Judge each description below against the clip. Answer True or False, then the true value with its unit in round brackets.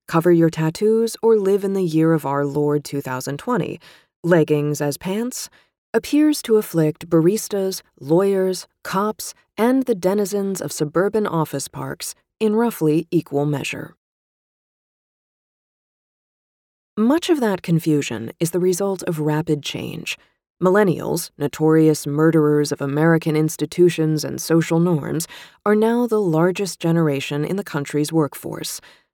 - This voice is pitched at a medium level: True (165 Hz)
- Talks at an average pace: False (125 wpm)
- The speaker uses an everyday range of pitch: True (4.6 semitones)